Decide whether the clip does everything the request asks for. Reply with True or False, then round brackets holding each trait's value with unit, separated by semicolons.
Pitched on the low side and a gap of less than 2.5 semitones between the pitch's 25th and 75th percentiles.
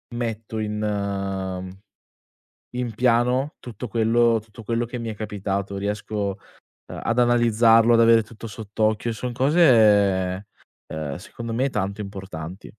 False (110 Hz; 2.9 semitones)